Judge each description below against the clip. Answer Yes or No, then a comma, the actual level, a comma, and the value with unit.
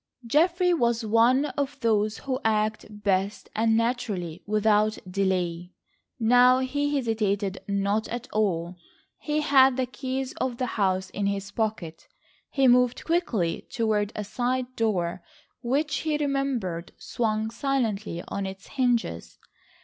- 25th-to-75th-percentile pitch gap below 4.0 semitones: No, average, 4.5 semitones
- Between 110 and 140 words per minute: Yes, slow, 135 wpm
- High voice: Yes, high, 225 Hz